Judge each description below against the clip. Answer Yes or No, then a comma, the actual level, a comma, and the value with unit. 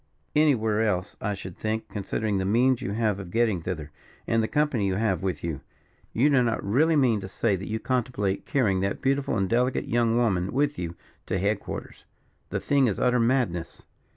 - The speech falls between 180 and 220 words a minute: Yes, average, 200 wpm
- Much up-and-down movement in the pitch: No, average, 4.6 semitones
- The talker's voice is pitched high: No, low, 110 Hz